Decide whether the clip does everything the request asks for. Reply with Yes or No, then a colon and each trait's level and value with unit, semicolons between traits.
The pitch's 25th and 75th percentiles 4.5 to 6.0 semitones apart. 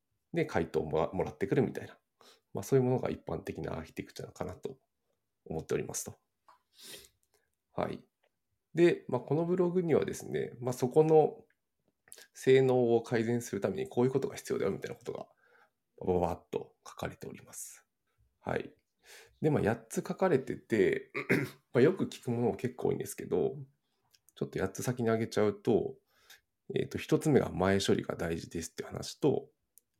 Yes: average, 5.2 semitones